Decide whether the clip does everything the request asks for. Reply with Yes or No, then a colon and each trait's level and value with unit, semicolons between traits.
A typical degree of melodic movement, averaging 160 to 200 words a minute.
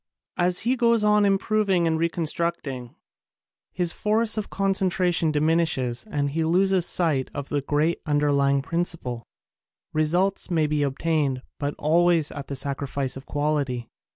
No: average, 4.2 semitones; average, 140 wpm